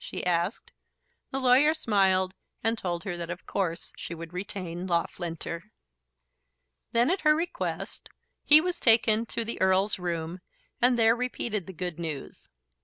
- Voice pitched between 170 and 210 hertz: Yes, high, 190 Hz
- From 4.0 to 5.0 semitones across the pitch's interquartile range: No, wide, 5.6 semitones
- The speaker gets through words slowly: No, average, 150 wpm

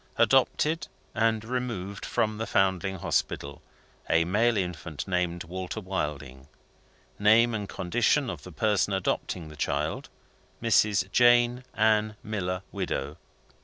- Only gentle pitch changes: No, average, 3.9 semitones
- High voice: No, low, 100 Hz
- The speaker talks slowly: Yes, slow, 120 wpm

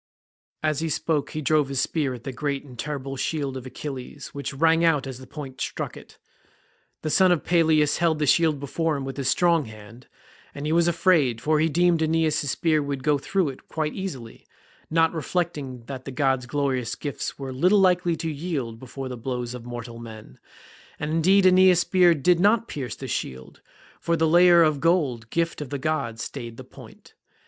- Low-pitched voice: No, medium, 150 Hz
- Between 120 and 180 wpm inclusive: No, average, 200 wpm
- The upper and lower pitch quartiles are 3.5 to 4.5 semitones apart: Yes, average, 4.0 semitones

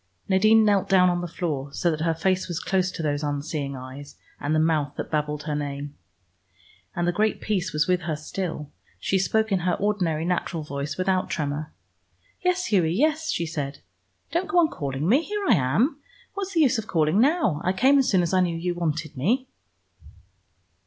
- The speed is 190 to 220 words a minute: Yes, average, 200 wpm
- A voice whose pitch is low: No, medium, 175 Hz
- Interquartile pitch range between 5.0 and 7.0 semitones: Yes, wide, 5.6 semitones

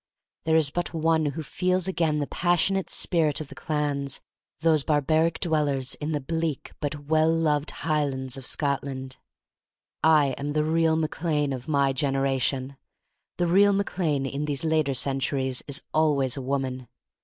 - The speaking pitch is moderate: Yes, medium, 150 Hz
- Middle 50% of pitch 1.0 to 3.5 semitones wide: Yes, average, 2.8 semitones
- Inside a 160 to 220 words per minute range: Yes, average, 165 wpm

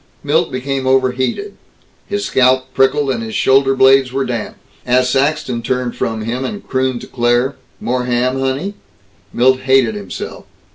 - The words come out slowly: No, average, 150 wpm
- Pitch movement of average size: No, narrow, 1.5 semitones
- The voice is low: Yes, low, 130 Hz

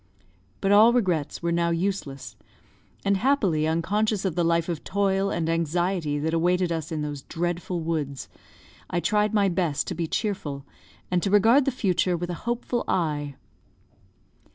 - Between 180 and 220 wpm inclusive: No, average, 160 wpm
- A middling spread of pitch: Yes, average, 3.5 semitones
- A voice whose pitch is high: No, medium, 175 Hz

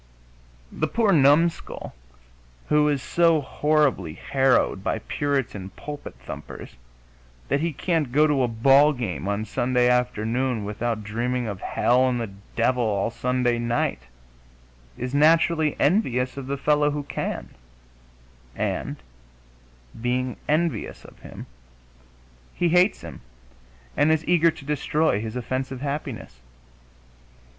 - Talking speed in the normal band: No, slow, 125 wpm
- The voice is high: No, low, 130 Hz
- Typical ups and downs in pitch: Yes, average, 4.1 semitones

